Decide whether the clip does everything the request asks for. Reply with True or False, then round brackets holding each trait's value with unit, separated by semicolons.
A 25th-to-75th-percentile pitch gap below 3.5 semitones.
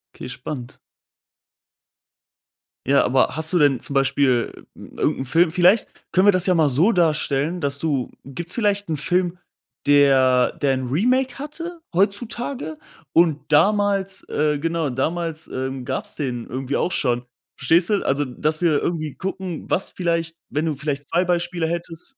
False (4.7 semitones)